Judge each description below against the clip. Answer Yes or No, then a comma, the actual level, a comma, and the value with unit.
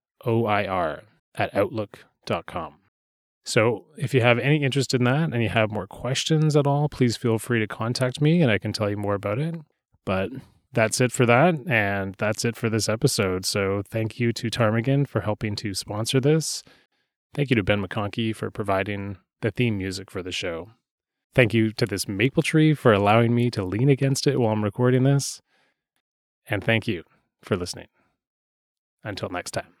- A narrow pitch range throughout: No, average, 4.2 semitones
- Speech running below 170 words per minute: No, average, 185 wpm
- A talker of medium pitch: No, low, 115 Hz